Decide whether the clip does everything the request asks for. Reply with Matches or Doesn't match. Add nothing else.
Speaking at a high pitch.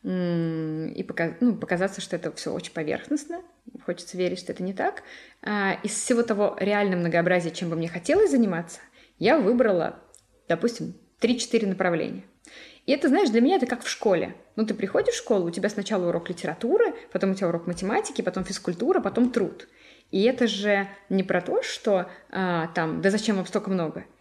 Matches